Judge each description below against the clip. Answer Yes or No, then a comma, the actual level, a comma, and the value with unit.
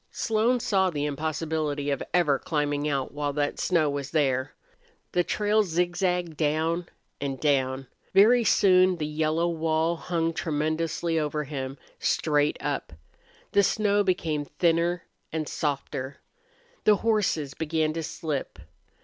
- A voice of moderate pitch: Yes, medium, 160 Hz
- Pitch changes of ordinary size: Yes, average, 3.3 semitones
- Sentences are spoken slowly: Yes, slow, 130 wpm